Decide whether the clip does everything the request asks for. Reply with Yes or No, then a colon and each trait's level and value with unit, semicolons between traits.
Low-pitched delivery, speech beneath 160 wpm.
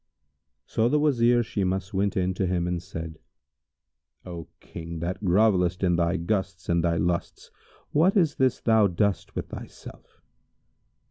Yes: very low, 95 Hz; average, 145 wpm